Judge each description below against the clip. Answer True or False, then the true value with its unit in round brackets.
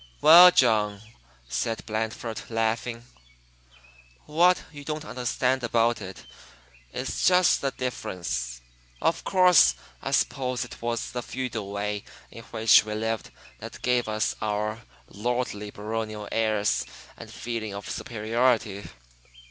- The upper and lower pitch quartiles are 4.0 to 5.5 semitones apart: False (2.9 semitones)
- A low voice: True (115 Hz)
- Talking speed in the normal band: False (120 wpm)